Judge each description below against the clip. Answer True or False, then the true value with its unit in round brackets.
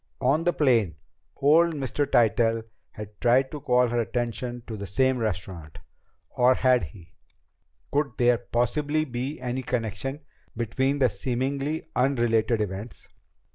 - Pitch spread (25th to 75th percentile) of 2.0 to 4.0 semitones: True (3.3 semitones)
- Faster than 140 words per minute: False (135 wpm)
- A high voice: False (125 Hz)